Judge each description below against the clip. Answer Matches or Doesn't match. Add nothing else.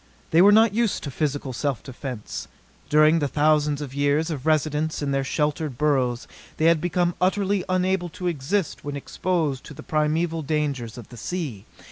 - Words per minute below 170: Doesn't match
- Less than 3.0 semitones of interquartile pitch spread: Doesn't match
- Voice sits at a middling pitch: Matches